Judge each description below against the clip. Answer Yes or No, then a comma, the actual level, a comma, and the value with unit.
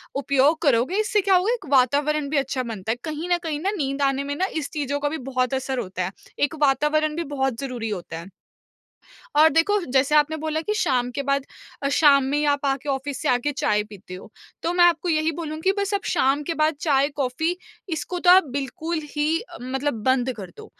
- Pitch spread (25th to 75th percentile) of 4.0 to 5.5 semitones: No, average, 3.2 semitones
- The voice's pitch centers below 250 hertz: No, very high, 285 Hz